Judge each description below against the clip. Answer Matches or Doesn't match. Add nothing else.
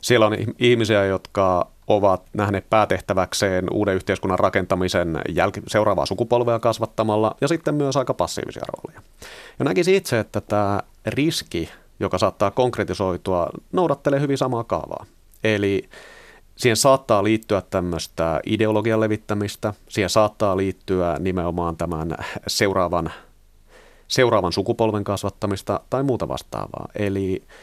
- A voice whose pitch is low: Matches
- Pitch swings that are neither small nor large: Matches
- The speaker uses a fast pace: Doesn't match